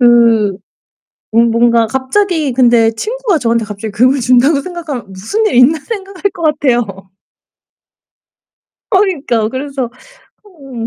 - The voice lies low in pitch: No, very high, 255 Hz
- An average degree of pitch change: No, wide, 5.8 semitones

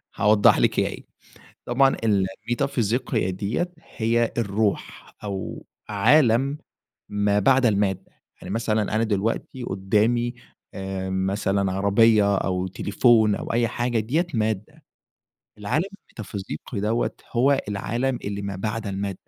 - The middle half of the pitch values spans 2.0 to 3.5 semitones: Yes, average, 3.1 semitones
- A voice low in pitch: Yes, low, 105 Hz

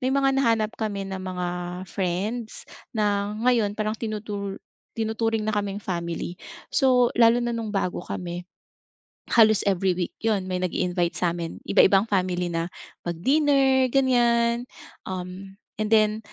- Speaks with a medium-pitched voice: No, high, 210 Hz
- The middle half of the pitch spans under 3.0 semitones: No, average, 4.1 semitones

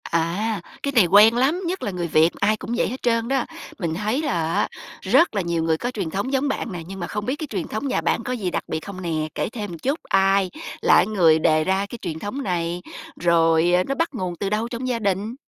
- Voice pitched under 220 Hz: Yes, high, 200 Hz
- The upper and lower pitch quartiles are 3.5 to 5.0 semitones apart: No, wide, 5.6 semitones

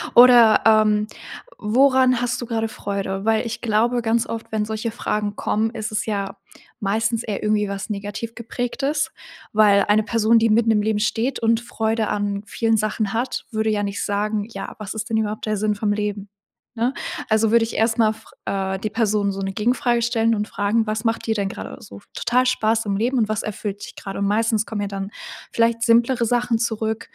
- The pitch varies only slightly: Yes, narrow, 1.8 semitones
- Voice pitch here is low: No, high, 220 Hz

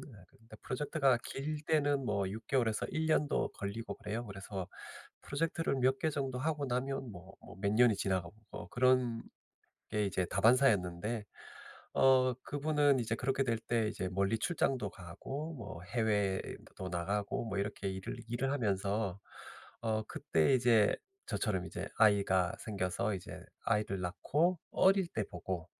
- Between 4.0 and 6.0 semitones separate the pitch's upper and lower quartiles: Yes, wide, 5.4 semitones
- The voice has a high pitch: No, low, 110 Hz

